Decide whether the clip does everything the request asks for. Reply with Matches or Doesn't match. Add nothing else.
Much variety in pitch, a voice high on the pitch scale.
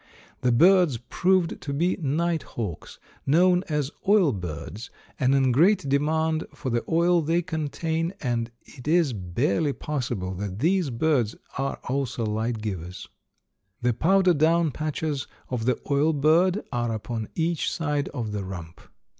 Doesn't match